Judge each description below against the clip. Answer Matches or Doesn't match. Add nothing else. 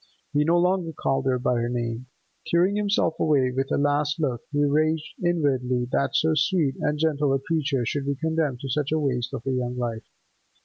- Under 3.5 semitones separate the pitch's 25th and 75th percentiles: Doesn't match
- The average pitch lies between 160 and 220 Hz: Doesn't match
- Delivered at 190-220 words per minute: Matches